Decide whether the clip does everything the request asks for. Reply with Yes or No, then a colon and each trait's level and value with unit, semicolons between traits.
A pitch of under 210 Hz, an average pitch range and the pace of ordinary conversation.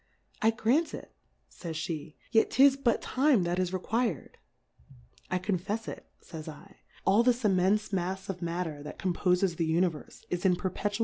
Yes: medium, 185 Hz; average, 4.4 semitones; average, 165 wpm